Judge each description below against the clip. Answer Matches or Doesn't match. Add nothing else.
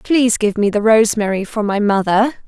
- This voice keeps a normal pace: Matches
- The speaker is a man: Doesn't match